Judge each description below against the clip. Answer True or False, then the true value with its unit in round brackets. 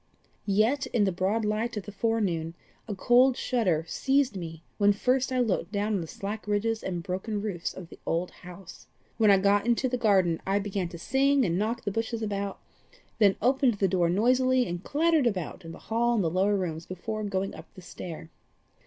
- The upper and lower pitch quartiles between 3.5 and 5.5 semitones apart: True (4.0 semitones)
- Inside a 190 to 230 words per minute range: True (205 wpm)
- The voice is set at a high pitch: True (205 Hz)